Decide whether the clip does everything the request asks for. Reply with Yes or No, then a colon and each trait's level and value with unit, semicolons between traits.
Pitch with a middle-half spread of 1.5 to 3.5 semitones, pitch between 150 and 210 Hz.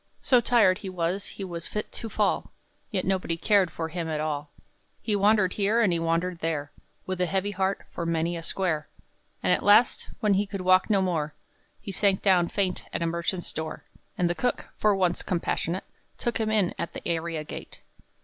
Yes: average, 3.1 semitones; medium, 185 Hz